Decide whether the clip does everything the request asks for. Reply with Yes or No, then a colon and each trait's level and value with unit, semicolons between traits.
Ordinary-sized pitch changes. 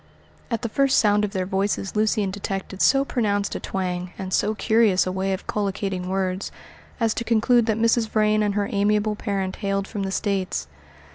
No: narrow, 2.2 semitones